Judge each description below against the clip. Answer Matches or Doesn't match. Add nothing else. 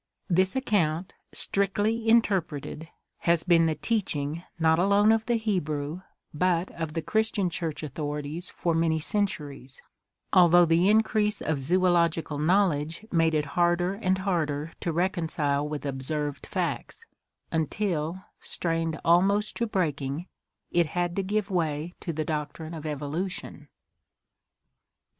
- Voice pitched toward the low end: Doesn't match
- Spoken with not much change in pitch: Doesn't match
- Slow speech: Matches